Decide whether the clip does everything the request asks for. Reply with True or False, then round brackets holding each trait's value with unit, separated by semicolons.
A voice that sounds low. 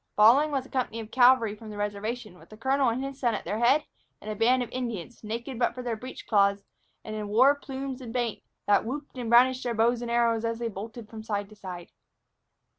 False (235 Hz)